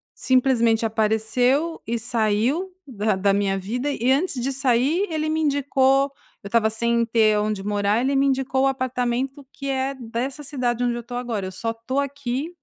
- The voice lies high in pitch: Yes, high, 245 Hz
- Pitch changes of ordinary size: Yes, average, 3.5 semitones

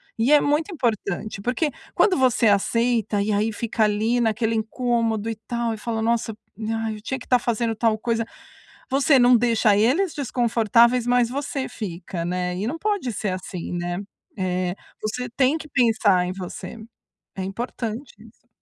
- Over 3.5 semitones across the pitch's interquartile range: No, average, 2.9 semitones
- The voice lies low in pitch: No, high, 230 Hz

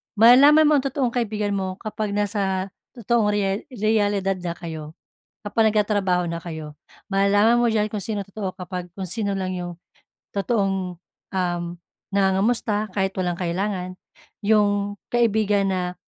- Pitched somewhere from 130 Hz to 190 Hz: No, high, 200 Hz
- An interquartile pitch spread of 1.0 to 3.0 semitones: Yes, narrow, 2.6 semitones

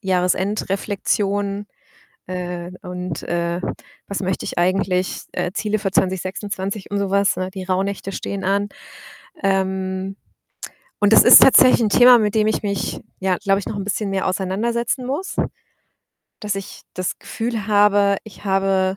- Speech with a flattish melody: Yes, narrow, 1.6 semitones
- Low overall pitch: No, high, 195 Hz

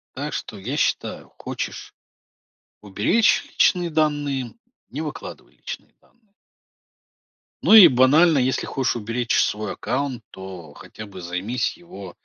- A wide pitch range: Yes, wide, 6.5 semitones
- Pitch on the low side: Yes, low, 130 Hz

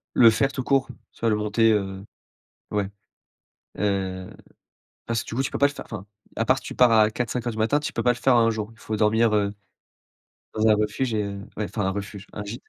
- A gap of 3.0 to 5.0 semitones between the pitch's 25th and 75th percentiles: No, narrow, 2.6 semitones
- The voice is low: Yes, low, 110 Hz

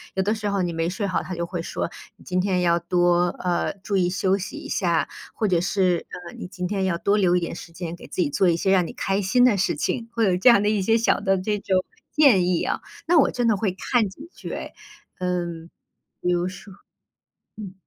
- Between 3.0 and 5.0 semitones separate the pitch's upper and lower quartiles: No, narrow, 2.5 semitones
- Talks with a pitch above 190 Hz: No, medium, 185 Hz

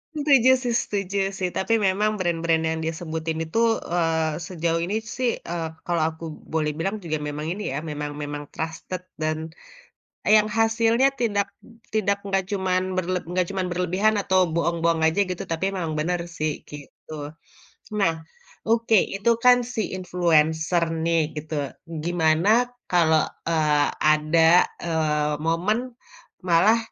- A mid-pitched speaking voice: Yes, medium, 170 Hz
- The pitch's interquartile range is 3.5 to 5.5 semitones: Yes, average, 3.9 semitones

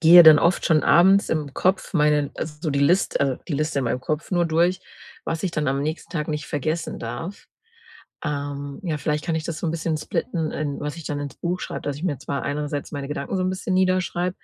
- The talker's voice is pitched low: No, medium, 155 Hz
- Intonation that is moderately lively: Yes, average, 3.1 semitones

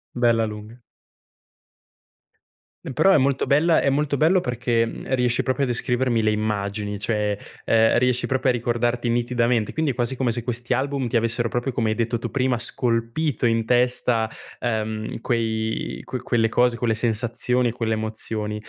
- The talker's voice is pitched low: Yes, low, 120 Hz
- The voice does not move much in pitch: Yes, narrow, 2.0 semitones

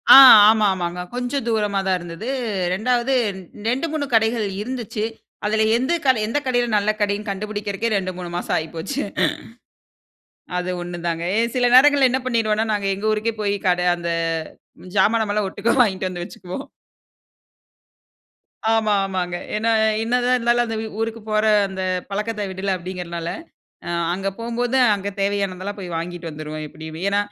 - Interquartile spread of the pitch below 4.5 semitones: Yes, average, 4.0 semitones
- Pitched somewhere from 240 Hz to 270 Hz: No, high, 210 Hz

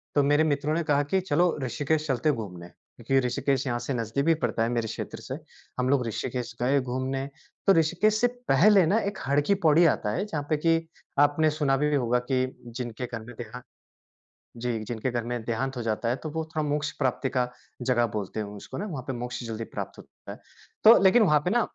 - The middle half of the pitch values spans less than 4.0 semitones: No, average, 4.3 semitones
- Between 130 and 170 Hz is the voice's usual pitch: Yes, low, 135 Hz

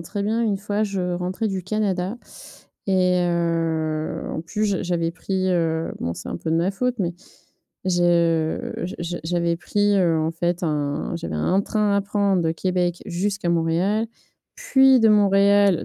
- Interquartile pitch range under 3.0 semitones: No, average, 3.3 semitones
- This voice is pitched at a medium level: Yes, medium, 180 Hz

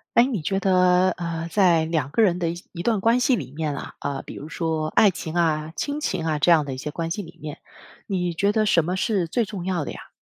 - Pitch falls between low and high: Yes, medium, 175 Hz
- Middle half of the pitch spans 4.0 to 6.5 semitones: No, average, 3.6 semitones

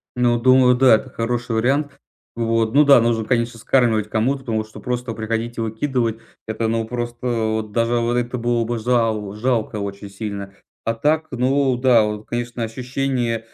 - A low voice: Yes, low, 115 Hz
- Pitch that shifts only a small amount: Yes, narrow, 2.0 semitones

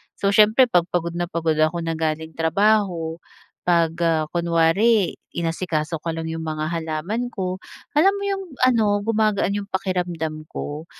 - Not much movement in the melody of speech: No, average, 4.0 semitones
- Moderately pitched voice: Yes, medium, 170 Hz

